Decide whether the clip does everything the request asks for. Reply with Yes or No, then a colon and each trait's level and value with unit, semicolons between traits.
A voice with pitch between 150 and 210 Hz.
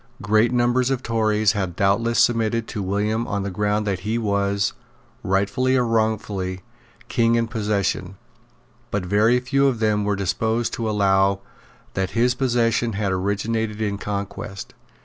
No: low, 105 Hz